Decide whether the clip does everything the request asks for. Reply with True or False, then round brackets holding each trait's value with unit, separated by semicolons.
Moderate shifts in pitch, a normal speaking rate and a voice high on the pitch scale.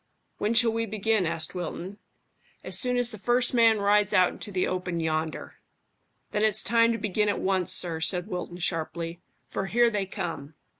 True (4.1 semitones; 185 wpm; 195 Hz)